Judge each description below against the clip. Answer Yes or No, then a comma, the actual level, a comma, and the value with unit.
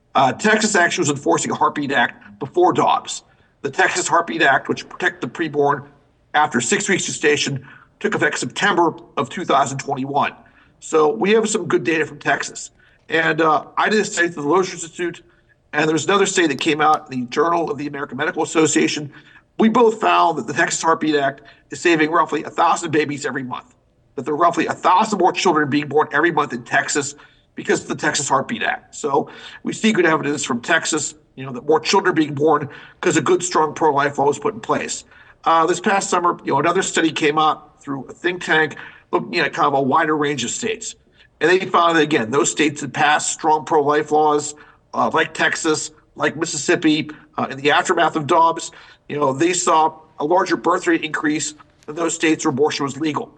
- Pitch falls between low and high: Yes, medium, 155 Hz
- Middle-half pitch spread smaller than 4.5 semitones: Yes, average, 2.8 semitones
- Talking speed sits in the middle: No, fast, 210 wpm